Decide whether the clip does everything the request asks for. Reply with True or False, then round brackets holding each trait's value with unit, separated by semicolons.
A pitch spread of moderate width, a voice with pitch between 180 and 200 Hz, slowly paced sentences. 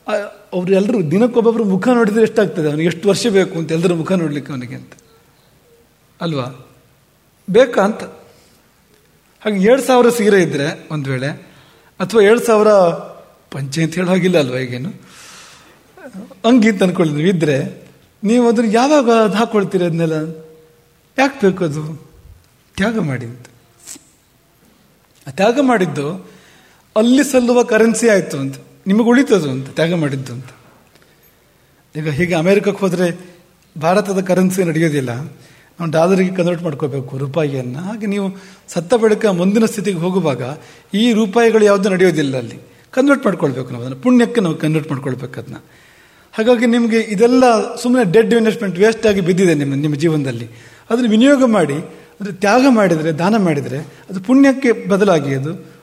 False (6.2 semitones; 185 Hz; 125 wpm)